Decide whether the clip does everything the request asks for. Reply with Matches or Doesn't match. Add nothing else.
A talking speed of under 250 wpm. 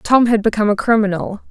Matches